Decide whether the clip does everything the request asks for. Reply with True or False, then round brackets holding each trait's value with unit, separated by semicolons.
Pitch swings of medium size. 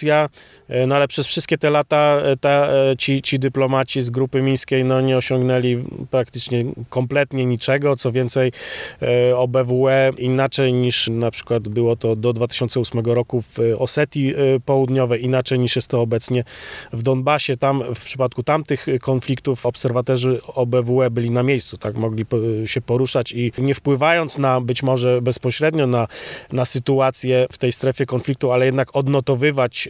False (1.7 semitones)